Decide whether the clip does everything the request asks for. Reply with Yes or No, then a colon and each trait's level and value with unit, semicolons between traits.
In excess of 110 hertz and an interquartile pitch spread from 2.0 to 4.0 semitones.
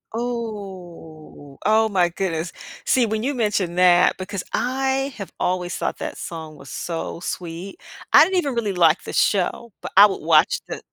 No: high, 190 Hz; average, 4.9 semitones